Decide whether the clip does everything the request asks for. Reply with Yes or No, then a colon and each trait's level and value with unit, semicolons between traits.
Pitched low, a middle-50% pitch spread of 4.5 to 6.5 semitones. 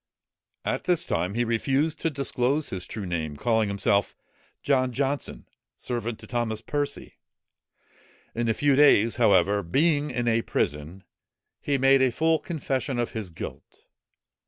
Yes: low, 120 Hz; average, 5.3 semitones